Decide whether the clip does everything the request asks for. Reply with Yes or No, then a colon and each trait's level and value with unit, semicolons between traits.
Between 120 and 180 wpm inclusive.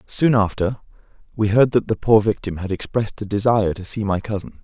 No: fast, 205 wpm